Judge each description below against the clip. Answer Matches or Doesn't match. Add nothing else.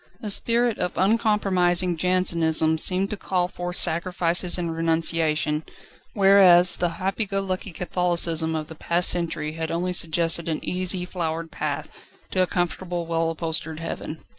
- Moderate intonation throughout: Doesn't match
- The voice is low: Doesn't match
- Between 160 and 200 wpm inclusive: Doesn't match